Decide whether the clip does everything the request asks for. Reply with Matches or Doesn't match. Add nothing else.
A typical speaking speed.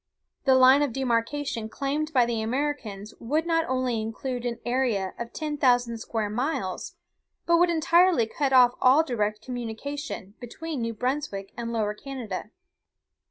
Matches